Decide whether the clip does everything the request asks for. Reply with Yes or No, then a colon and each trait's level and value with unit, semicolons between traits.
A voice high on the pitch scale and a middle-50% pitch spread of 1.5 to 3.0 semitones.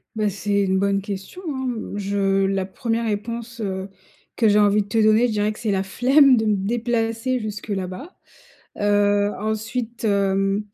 Yes: high, 210 Hz; narrow, 2.6 semitones